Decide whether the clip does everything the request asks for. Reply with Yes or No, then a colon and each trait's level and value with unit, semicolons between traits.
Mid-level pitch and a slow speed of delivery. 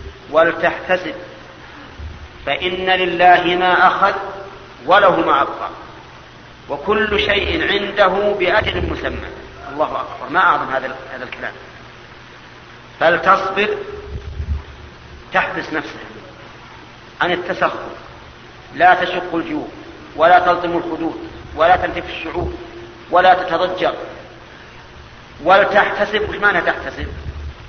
Yes: medium, 180 Hz; slow, 80 wpm